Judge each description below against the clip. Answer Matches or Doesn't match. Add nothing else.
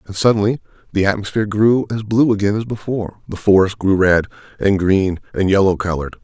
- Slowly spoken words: Doesn't match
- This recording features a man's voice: Matches